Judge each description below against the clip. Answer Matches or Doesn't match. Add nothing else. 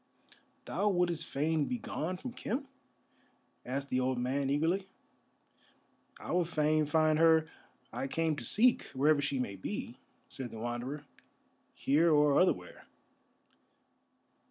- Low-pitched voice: Doesn't match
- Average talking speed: Doesn't match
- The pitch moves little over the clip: Doesn't match